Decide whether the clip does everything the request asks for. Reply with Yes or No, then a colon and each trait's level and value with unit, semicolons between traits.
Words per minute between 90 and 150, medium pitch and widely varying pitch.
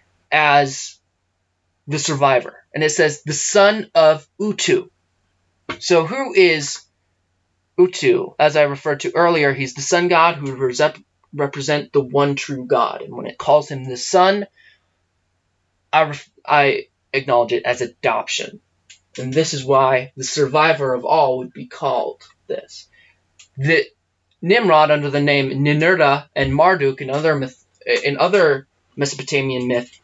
No: average, 140 wpm; medium, 145 Hz; average, 3.9 semitones